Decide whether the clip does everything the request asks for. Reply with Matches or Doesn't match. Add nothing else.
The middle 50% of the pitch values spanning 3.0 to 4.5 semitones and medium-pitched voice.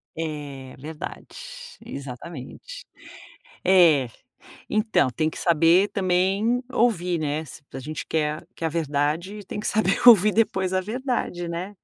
Doesn't match